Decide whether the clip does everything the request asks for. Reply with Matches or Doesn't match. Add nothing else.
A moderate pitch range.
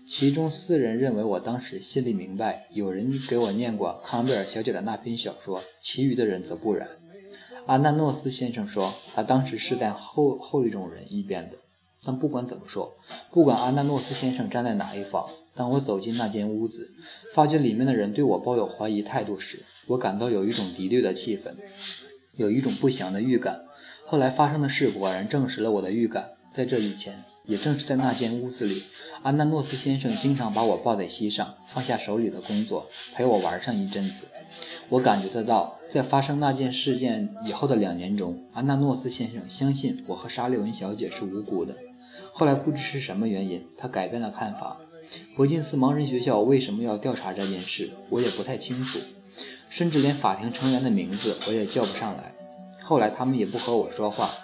Doesn't match